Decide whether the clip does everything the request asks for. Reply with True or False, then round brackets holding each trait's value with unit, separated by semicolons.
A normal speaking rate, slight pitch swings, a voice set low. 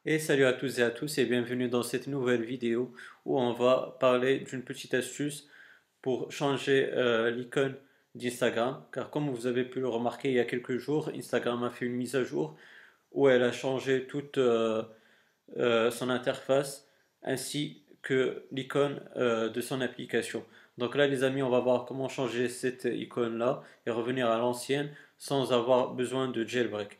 True (180 wpm; 1.9 semitones; 125 Hz)